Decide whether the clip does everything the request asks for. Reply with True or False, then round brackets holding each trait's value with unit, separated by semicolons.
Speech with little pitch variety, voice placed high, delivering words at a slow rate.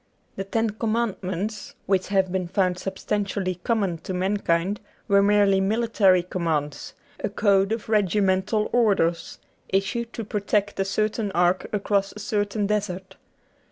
True (2.0 semitones; 200 Hz; 130 wpm)